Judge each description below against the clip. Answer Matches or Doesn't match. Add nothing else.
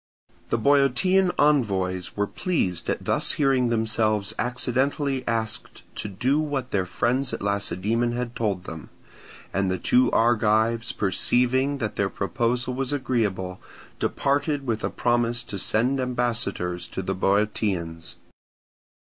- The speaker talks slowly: Matches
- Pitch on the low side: Matches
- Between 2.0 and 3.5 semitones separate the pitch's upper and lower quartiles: Doesn't match